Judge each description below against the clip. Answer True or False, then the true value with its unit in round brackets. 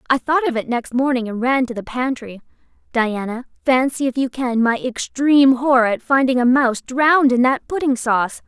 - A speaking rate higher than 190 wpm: True (200 wpm)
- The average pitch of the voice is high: True (255 Hz)